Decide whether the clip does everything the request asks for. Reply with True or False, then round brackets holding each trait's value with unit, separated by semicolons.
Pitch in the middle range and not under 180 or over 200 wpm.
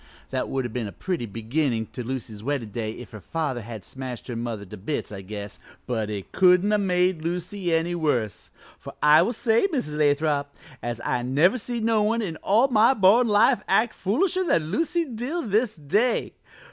True (160 Hz; 195 wpm)